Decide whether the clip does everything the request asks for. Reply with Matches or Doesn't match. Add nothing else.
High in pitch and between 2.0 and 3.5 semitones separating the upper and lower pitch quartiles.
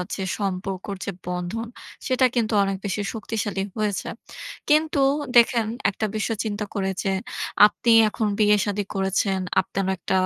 Matches